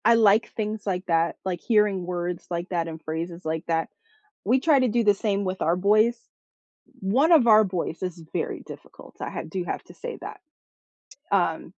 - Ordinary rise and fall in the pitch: Yes, average, 4.0 semitones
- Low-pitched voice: No, high, 190 Hz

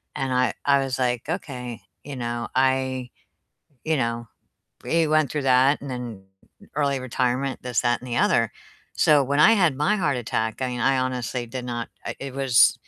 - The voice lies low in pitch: Yes, low, 130 Hz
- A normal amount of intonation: No, narrow, 2.3 semitones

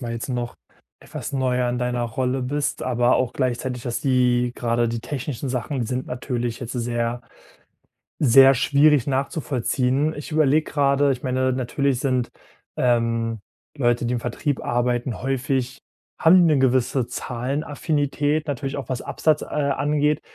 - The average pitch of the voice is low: Yes, low, 130 Hz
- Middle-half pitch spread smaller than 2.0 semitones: No, narrow, 2.5 semitones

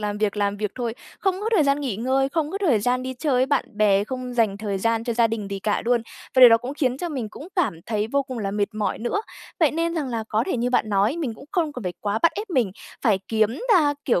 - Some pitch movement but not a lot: Yes, average, 4.8 semitones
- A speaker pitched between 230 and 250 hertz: Yes, high, 240 Hz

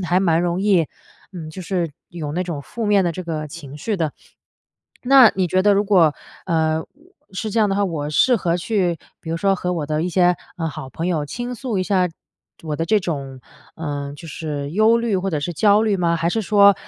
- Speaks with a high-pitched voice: No, medium, 175 Hz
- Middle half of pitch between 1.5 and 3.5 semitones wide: No, average, 4.0 semitones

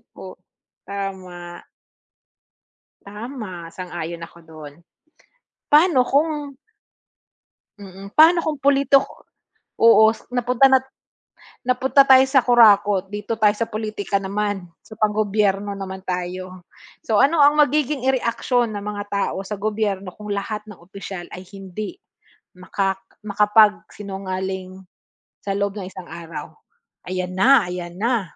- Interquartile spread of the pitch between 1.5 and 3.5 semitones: No, average, 4.1 semitones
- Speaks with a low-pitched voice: No, high, 205 Hz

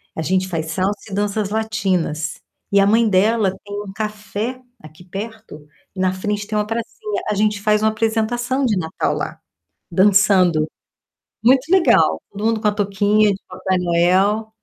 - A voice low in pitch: No, high, 205 Hz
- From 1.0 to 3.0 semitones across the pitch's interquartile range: Yes, average, 2.7 semitones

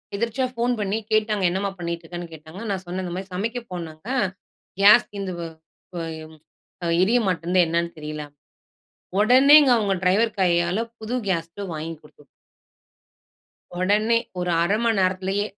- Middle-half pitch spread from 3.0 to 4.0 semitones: Yes, average, 3.7 semitones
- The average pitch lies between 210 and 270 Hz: No, high, 190 Hz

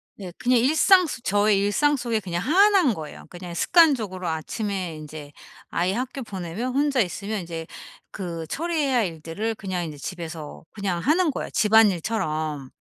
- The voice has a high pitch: Yes, high, 200 Hz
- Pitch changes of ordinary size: No, wide, 6.9 semitones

